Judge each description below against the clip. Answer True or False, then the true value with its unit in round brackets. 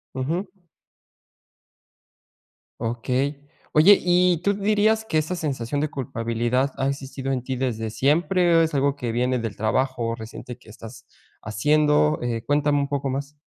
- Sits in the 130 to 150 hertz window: True (140 Hz)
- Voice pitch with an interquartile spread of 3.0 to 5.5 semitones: True (4.1 semitones)